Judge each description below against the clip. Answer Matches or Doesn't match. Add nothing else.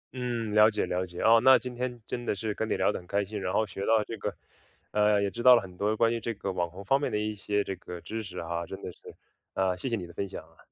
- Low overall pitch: Matches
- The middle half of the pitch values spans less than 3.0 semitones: Doesn't match